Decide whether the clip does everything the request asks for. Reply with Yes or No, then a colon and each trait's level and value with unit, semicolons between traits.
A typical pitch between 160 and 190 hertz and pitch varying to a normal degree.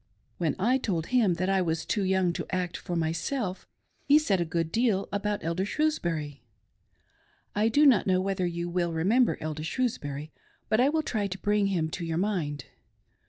Yes: medium, 185 Hz; average, 4.2 semitones